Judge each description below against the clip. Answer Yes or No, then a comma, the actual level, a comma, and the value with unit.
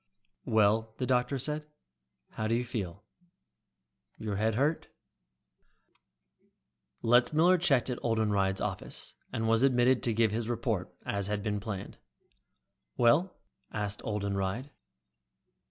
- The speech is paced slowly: Yes, slow, 115 wpm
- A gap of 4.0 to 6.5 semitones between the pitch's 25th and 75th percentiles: No, average, 3.2 semitones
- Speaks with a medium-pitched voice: No, low, 115 Hz